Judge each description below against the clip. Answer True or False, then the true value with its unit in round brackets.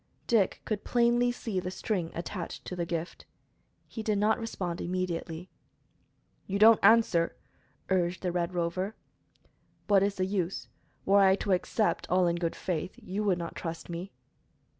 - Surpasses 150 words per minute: True (160 wpm)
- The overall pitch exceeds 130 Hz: True (185 Hz)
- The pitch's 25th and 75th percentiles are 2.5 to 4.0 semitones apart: True (3.1 semitones)